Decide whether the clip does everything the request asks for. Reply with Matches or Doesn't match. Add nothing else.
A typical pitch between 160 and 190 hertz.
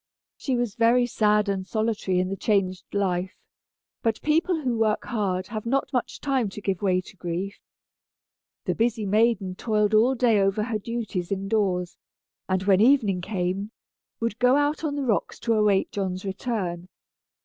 Doesn't match